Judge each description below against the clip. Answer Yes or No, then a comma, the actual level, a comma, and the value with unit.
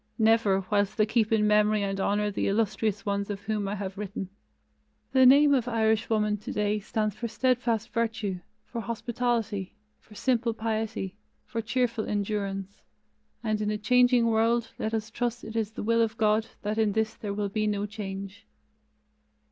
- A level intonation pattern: Yes, narrow, 1.8 semitones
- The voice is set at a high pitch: Yes, high, 215 Hz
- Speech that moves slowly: No, average, 170 wpm